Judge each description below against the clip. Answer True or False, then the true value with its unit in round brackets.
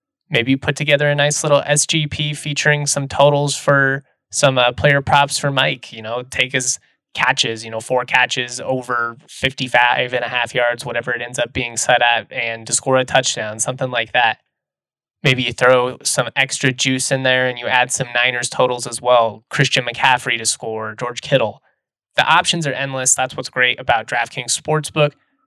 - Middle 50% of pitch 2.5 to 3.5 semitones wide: True (2.8 semitones)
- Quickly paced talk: False (190 wpm)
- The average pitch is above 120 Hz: True (130 Hz)